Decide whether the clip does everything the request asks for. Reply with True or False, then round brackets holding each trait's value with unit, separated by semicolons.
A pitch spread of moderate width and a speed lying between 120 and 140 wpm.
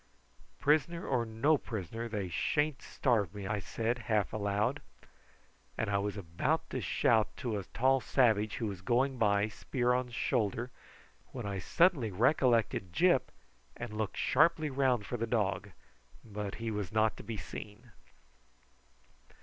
False (3.6 semitones; 150 wpm)